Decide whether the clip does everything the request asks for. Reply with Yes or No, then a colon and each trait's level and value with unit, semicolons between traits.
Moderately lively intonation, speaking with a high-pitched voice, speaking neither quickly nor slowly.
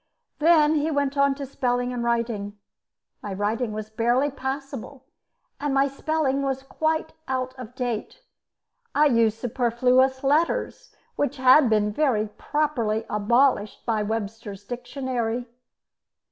No: average, 3.8 semitones; very high, 255 Hz; slow, 125 wpm